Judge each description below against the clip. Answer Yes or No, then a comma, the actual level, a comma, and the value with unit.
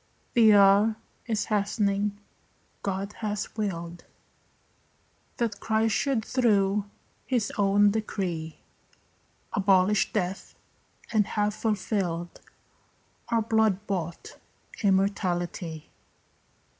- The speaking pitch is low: No, high, 205 Hz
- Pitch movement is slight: Yes, narrow, 2.2 semitones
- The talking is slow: Yes, slow, 80 wpm